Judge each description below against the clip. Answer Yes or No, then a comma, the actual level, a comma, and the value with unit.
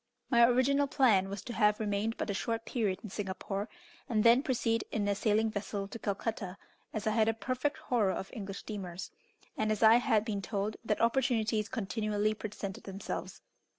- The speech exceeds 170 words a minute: Yes, average, 185 wpm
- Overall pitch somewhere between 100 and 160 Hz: No, high, 215 Hz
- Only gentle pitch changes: Yes, narrow, 2.3 semitones